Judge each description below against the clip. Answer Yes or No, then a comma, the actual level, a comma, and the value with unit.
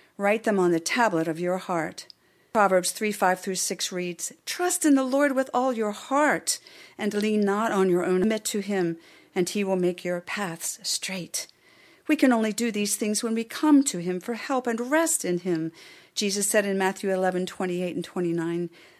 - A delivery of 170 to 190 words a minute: No, fast, 205 wpm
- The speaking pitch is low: No, high, 205 Hz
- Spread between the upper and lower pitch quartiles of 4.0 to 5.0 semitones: Yes, average, 4.6 semitones